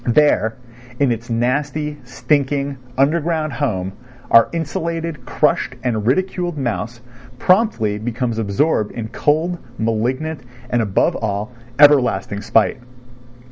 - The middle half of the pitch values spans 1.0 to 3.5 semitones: No, average, 5.1 semitones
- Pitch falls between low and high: No, low, 130 Hz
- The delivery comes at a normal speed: No, slow, 105 wpm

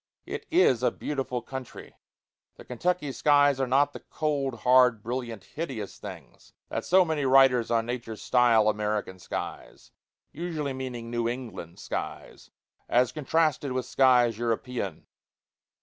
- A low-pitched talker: Yes, low, 125 Hz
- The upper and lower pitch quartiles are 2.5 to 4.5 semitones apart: Yes, average, 3.3 semitones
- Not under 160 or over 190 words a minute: No, slow, 135 wpm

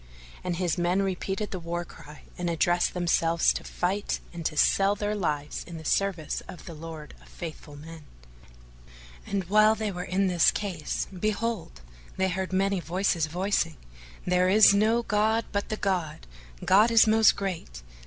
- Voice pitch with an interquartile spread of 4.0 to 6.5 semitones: No, average, 3.3 semitones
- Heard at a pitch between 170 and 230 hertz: Yes, medium, 185 Hz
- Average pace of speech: Yes, average, 165 wpm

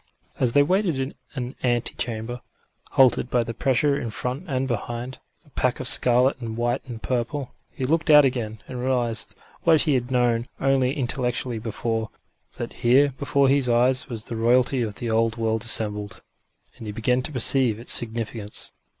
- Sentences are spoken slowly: No, average, 175 wpm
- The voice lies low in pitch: Yes, low, 125 Hz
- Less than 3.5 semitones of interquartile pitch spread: Yes, narrow, 2.4 semitones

